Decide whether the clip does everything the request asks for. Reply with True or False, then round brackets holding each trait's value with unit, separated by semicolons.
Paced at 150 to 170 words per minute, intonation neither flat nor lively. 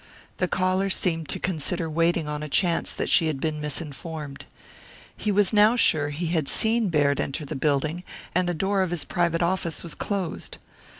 False (185 wpm; 3.4 semitones)